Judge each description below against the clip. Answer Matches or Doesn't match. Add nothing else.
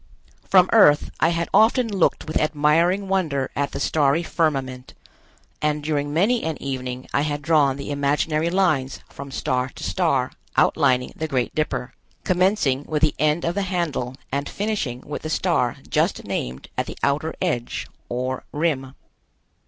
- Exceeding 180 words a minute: Doesn't match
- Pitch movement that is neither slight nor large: Matches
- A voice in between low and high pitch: Matches